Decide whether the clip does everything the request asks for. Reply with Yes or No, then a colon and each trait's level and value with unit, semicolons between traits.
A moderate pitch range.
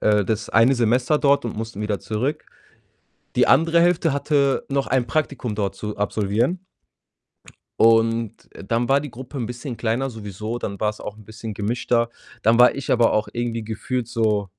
Yes: average, 3.6 semitones